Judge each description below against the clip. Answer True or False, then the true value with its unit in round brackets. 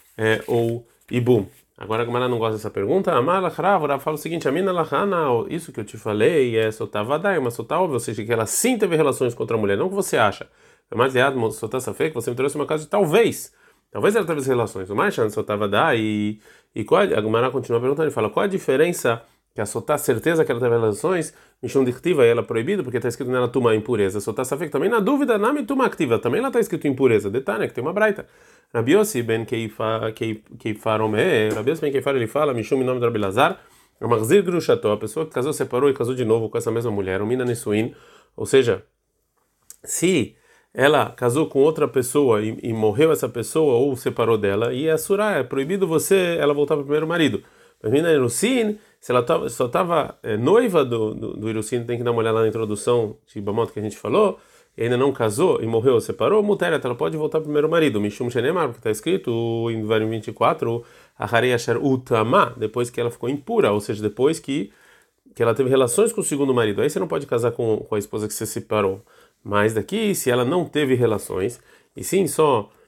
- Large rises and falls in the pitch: True (5.8 semitones)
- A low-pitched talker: True (125 Hz)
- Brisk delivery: True (220 wpm)